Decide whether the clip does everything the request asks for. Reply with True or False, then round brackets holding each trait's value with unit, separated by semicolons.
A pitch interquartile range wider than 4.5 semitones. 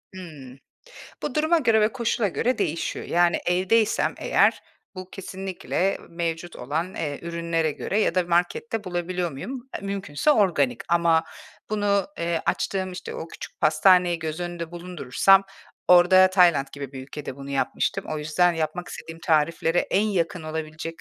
False (3.0 semitones)